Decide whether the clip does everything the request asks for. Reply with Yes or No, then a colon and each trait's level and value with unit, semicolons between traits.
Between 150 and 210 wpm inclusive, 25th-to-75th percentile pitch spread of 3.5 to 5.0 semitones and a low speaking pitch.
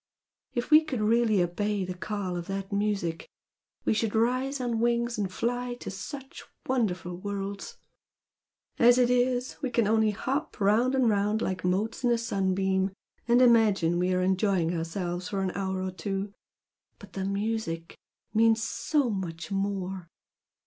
No: average, 155 wpm; average, 3.9 semitones; high, 205 Hz